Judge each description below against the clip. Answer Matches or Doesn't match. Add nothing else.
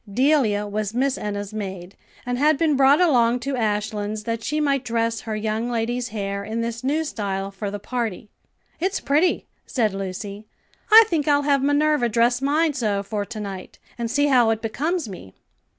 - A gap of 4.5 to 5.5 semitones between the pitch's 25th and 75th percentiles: Matches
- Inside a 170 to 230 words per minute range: Matches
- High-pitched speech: Matches